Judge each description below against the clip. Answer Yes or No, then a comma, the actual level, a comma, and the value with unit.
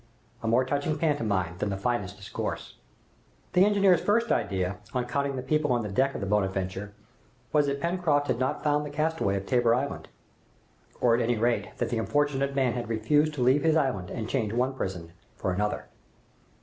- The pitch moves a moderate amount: No, wide, 5.9 semitones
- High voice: No, low, 125 Hz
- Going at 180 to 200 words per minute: Yes, average, 190 wpm